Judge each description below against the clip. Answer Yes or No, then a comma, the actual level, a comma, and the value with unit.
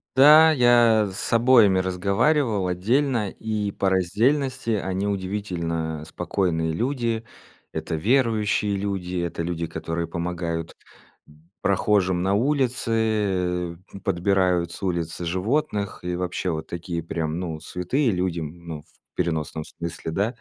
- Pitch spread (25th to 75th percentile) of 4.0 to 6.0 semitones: Yes, average, 4.6 semitones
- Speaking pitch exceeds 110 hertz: No, very low, 95 Hz